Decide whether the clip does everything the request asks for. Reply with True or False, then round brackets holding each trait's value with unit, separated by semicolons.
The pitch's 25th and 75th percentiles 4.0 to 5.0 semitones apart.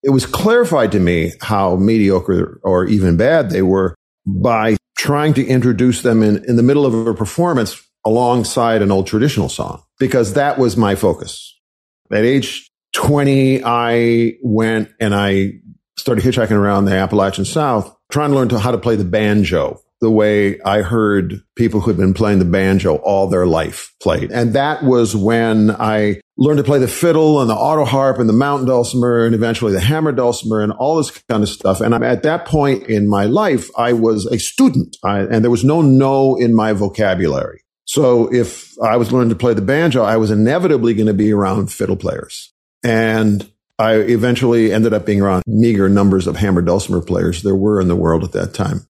False (3.5 semitones)